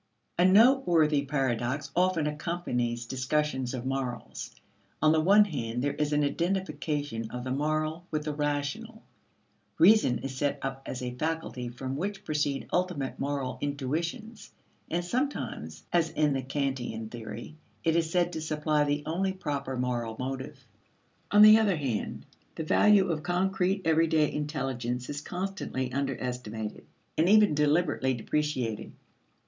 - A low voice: No, medium, 150 Hz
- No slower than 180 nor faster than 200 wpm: No, average, 140 wpm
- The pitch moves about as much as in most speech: Yes, average, 4.7 semitones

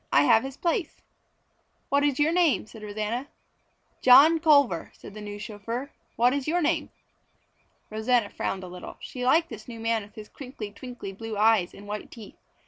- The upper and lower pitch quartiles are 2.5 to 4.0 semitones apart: No, average, 5.0 semitones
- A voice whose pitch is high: Yes, high, 230 Hz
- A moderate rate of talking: Yes, average, 180 wpm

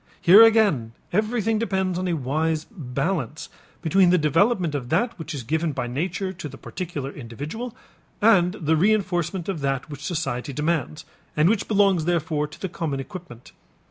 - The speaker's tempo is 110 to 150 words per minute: No, average, 165 wpm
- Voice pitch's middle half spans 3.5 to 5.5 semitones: Yes, average, 4.8 semitones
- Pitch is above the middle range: No, medium, 165 Hz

